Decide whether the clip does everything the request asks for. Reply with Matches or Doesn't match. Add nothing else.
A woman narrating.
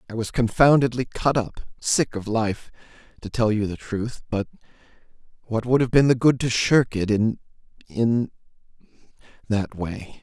Doesn't match